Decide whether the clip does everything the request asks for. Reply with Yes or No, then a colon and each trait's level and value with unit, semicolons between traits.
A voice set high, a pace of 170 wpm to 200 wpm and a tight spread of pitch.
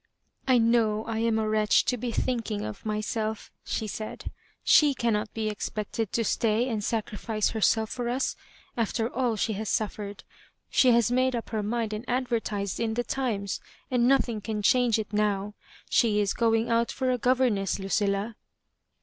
Yes: high, 220 Hz; average, 185 wpm; narrow, 2.2 semitones